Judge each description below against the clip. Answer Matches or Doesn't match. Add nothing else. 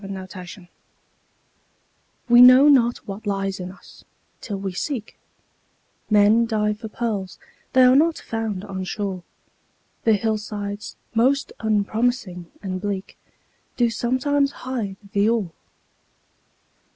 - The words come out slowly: Matches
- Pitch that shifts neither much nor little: Matches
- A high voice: Matches